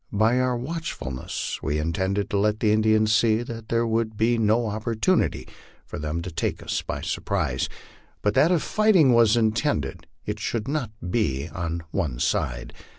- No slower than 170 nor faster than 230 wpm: Yes, average, 175 wpm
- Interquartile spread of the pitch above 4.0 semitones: Yes, average, 4.4 semitones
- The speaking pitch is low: Yes, low, 110 Hz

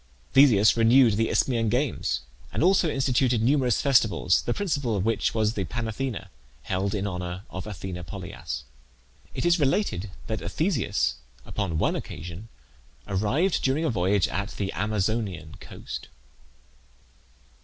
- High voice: No, low, 110 Hz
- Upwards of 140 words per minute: No, slow, 135 wpm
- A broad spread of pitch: Yes, wide, 5.7 semitones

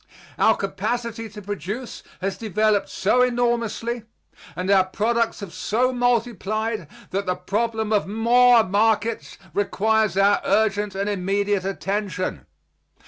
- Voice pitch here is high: Yes, high, 215 Hz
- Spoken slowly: Yes, slow, 120 wpm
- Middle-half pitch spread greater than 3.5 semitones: No, average, 2.7 semitones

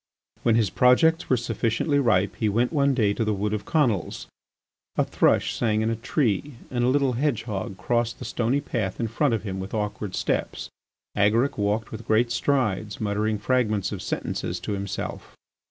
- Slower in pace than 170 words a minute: No, average, 180 wpm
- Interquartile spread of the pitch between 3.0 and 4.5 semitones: Yes, average, 3.3 semitones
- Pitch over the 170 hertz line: No, low, 115 Hz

